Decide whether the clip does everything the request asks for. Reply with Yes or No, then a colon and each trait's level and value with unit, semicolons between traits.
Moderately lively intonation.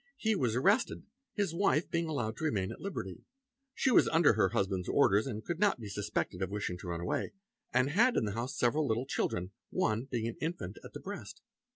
No: wide, 8.5 semitones